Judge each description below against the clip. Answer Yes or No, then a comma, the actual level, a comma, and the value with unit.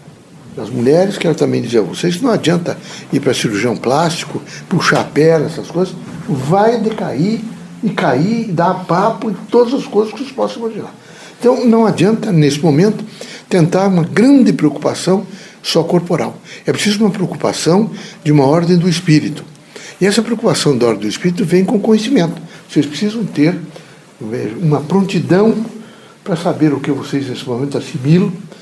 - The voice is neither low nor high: Yes, medium, 180 Hz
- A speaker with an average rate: Yes, average, 160 wpm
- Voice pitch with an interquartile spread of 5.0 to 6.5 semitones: Yes, wide, 5.5 semitones